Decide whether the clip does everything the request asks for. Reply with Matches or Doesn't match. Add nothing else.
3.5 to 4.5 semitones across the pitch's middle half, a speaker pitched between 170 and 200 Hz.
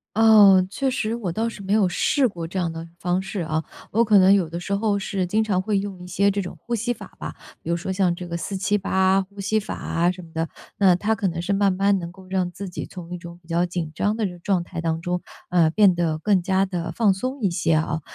Doesn't match